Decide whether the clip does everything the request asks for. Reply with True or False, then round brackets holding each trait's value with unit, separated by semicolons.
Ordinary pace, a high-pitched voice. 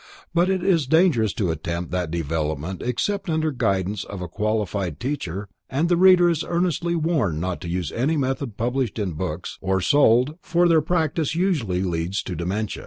False (175 wpm; 115 Hz)